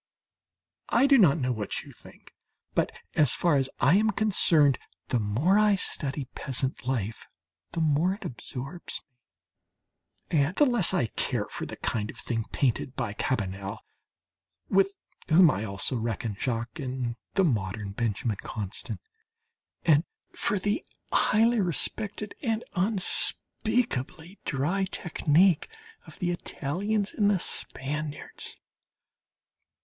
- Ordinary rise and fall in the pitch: No, wide, 8.2 semitones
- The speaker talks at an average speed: No, slow, 130 wpm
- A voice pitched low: No, medium, 150 Hz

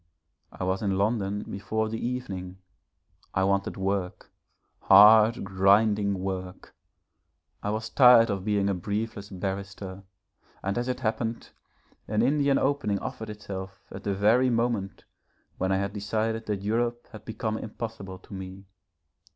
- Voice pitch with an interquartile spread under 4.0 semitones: Yes, narrow, 2.6 semitones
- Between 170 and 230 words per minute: No, average, 140 wpm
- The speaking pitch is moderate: No, low, 105 Hz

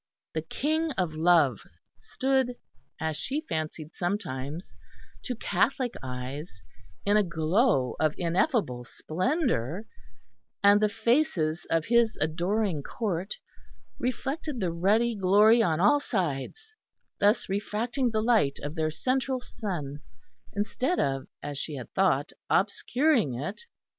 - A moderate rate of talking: No, slow, 120 wpm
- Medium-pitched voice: No, high, 195 Hz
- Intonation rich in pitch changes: Yes, wide, 7.4 semitones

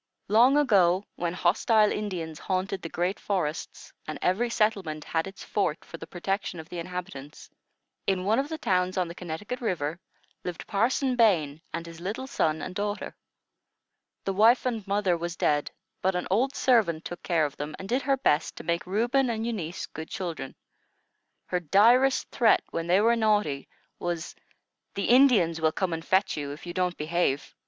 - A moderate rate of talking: Yes, average, 180 wpm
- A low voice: No, medium, 185 Hz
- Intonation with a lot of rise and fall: No, average, 4.6 semitones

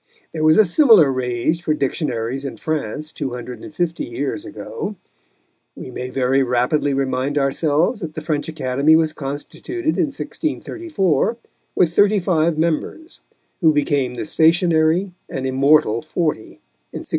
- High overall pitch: No, medium, 155 Hz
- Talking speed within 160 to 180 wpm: No, average, 145 wpm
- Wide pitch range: No, average, 4.1 semitones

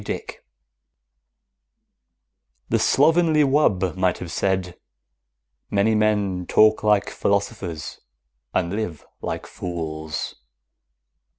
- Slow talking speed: Yes, slow, 90 wpm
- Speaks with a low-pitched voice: Yes, low, 100 Hz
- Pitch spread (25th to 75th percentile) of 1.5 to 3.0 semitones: No, average, 3.4 semitones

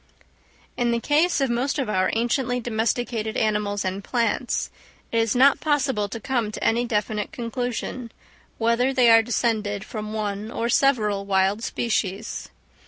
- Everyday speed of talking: Yes, average, 150 wpm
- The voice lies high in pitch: Yes, high, 230 Hz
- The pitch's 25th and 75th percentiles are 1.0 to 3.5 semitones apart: Yes, average, 2.8 semitones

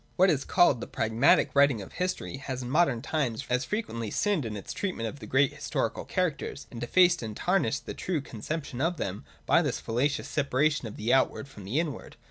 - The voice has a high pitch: No, low, 135 Hz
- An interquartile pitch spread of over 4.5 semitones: Yes, average, 5.2 semitones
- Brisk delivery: Yes, fast, 210 wpm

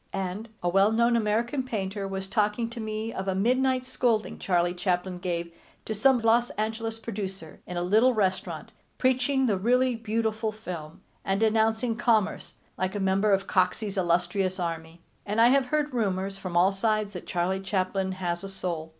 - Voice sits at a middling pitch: No, high, 205 Hz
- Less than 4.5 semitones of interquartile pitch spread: Yes, average, 3.5 semitones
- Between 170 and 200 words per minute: Yes, average, 175 wpm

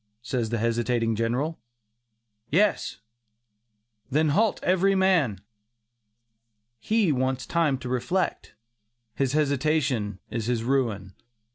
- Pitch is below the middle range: Yes, low, 130 Hz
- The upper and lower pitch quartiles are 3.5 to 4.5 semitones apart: No, wide, 5.5 semitones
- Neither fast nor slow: No, slow, 100 wpm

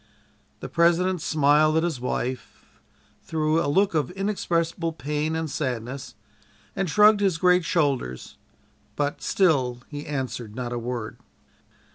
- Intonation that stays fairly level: No, average, 4.8 semitones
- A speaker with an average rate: No, slow, 130 wpm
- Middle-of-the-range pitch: Yes, medium, 155 Hz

